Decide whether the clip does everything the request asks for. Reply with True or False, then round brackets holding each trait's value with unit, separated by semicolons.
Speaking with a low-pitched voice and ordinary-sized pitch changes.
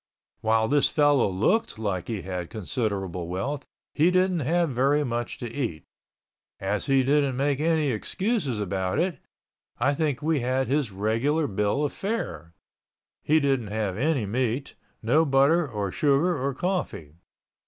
False (130 Hz; 6.0 semitones)